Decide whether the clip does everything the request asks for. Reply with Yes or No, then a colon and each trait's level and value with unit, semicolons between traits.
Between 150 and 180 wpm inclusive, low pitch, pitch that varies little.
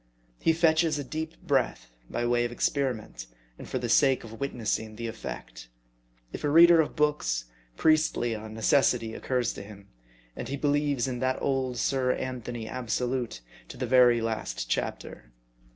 No: average, 160 wpm; low, 125 Hz; average, 3.9 semitones